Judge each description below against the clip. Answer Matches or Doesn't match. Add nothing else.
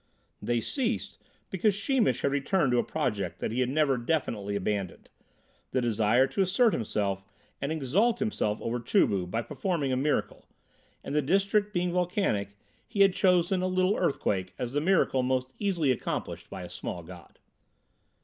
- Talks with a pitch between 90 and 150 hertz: Matches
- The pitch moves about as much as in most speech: Doesn't match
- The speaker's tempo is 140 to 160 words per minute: Doesn't match